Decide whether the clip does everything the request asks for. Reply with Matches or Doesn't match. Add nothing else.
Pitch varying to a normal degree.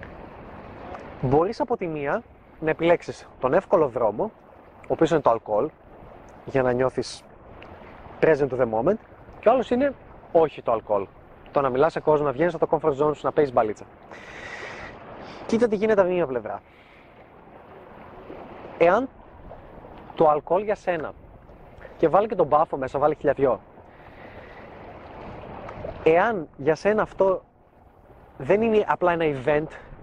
Matches